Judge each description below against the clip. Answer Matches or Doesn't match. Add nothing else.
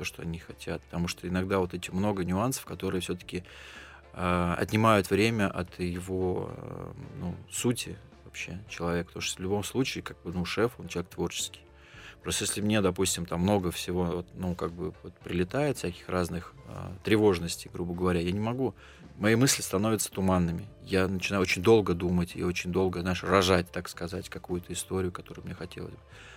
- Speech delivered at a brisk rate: Matches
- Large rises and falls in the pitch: Doesn't match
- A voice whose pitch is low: Matches